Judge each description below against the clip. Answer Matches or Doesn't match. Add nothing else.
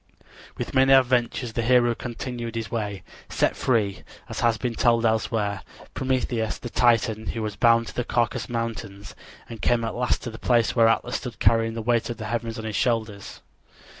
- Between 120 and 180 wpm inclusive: Doesn't match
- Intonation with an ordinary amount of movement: Doesn't match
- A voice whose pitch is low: Matches